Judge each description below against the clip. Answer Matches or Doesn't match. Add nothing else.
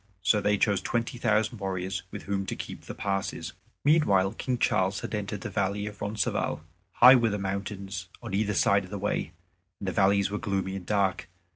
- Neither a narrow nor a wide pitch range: Doesn't match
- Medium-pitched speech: Doesn't match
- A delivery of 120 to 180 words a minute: Doesn't match